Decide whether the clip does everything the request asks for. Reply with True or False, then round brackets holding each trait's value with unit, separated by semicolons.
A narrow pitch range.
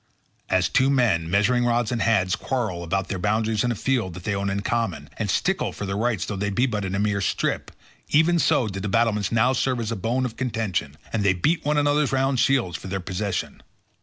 False (4.1 semitones)